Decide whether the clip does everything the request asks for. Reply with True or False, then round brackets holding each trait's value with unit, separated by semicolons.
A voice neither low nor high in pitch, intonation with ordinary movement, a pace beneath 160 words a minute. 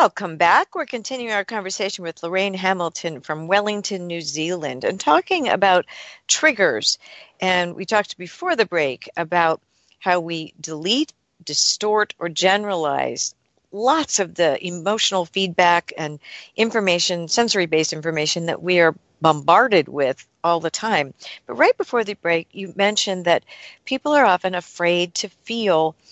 True (180 Hz; 3.8 semitones; 140 wpm)